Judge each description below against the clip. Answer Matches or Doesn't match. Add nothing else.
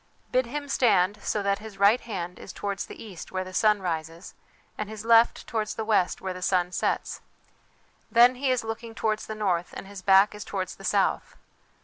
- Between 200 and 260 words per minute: Matches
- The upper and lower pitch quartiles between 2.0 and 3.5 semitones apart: Matches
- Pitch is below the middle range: Doesn't match